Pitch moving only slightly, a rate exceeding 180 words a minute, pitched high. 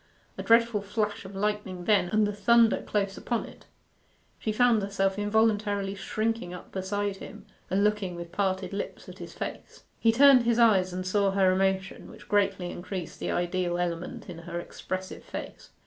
No: narrow, 2.3 semitones; average, 175 wpm; high, 200 Hz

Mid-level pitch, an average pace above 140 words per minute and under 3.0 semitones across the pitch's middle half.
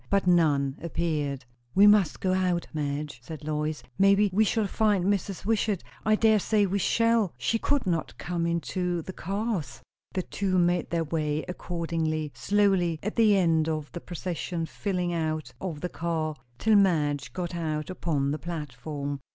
No: medium, 170 Hz; average, 170 wpm; average, 4.1 semitones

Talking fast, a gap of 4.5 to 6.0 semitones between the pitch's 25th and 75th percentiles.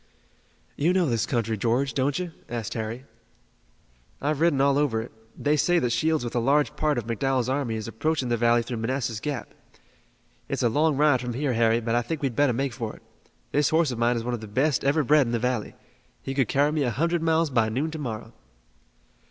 No: fast, 225 wpm; average, 4.0 semitones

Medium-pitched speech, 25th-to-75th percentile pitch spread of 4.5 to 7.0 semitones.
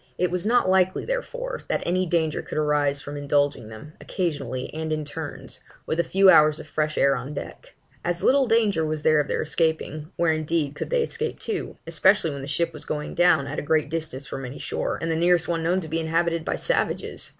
No: medium, 160 Hz; average, 3.2 semitones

